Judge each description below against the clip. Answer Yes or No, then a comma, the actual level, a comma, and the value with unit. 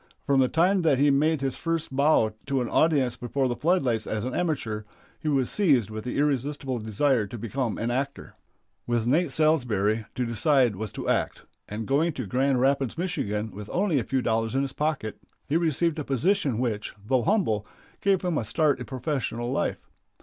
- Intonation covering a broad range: No, average, 4.7 semitones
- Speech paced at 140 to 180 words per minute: No, average, 195 wpm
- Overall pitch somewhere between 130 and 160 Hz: Yes, low, 135 Hz